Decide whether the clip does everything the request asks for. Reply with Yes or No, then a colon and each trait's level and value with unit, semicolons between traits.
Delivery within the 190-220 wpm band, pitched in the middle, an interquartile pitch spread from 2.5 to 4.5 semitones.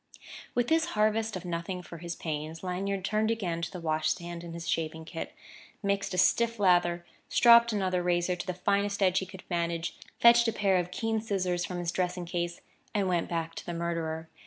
Yes: fast, 205 wpm; medium, 180 Hz; average, 2.9 semitones